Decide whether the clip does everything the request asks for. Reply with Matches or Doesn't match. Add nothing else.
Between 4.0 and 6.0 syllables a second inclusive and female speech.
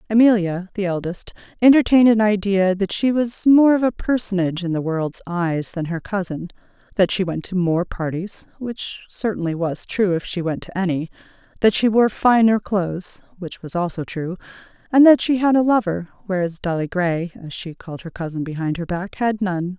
Matches